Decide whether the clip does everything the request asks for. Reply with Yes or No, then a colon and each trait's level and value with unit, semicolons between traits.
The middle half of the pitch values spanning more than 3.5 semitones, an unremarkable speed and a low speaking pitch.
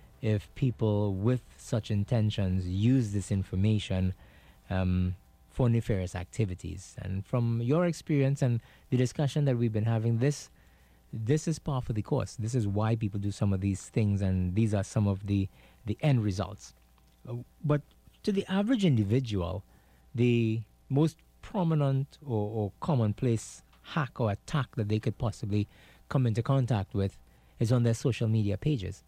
Yes: average, 4.6 semitones; average, 155 wpm; low, 110 Hz